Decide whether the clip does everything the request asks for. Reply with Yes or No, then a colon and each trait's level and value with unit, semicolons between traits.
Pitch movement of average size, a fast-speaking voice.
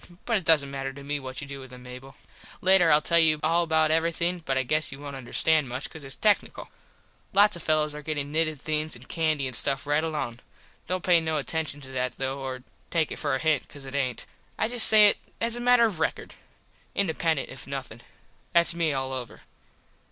Yes: average, 3.6 semitones; fast, 225 wpm